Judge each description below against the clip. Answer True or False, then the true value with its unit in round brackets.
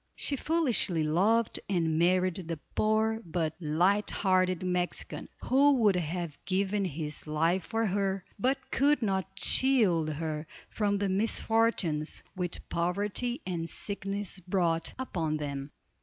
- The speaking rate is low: True (125 wpm)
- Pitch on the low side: False (185 Hz)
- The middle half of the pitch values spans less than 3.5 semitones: False (4.4 semitones)